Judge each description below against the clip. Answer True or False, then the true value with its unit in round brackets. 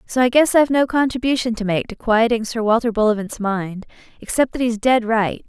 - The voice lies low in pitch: False (230 Hz)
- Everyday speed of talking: False (210 wpm)